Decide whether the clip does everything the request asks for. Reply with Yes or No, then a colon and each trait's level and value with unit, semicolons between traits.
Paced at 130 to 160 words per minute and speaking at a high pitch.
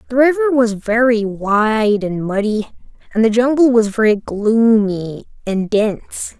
Yes: average, 140 wpm; high, 220 Hz